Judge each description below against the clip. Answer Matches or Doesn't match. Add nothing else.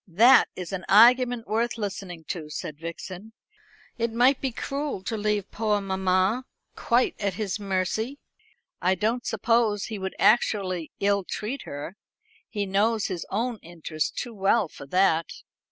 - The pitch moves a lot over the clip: Doesn't match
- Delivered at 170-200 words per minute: Doesn't match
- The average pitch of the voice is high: Matches